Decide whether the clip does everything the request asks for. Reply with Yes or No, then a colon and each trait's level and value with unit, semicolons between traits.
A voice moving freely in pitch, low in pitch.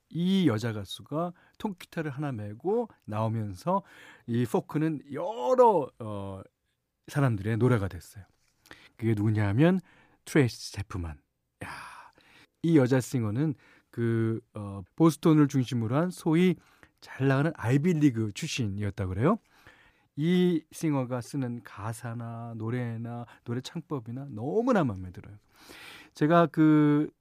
Yes: wide, 6.2 semitones; low, 130 Hz